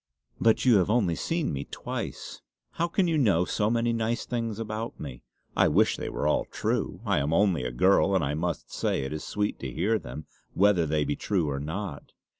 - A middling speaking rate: No, fast, 215 wpm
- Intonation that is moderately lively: No, wide, 7.1 semitones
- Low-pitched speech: Yes, very low, 95 Hz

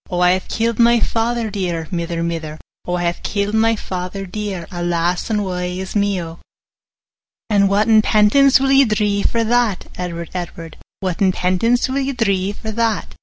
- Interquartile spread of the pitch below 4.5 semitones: Yes, average, 4.0 semitones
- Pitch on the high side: Yes, high, 200 Hz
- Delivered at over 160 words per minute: Yes, average, 185 wpm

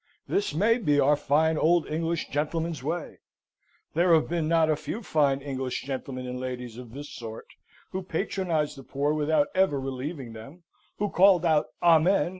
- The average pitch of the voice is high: No, medium, 155 Hz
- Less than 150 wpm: No, average, 170 wpm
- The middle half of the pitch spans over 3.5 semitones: Yes, average, 3.9 semitones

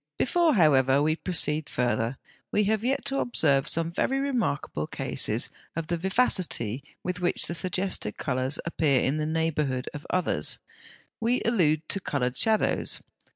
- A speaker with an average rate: Yes, average, 150 wpm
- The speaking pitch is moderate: Yes, medium, 165 Hz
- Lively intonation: Yes, wide, 6.1 semitones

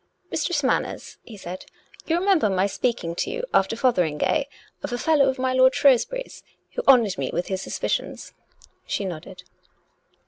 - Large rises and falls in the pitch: Yes, wide, 7.0 semitones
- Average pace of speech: Yes, average, 180 wpm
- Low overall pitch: No, high, 245 Hz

